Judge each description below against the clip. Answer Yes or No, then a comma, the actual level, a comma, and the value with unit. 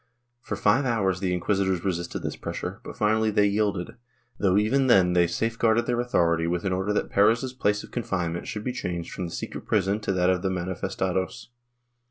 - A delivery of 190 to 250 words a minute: Yes, average, 195 wpm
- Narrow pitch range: No, average, 3.5 semitones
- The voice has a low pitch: Yes, low, 100 Hz